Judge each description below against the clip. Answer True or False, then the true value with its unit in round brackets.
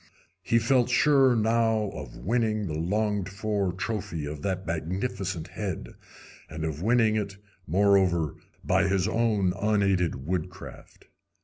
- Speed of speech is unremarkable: False (125 wpm)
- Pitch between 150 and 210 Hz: False (100 Hz)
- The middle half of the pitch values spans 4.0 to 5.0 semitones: False (3.6 semitones)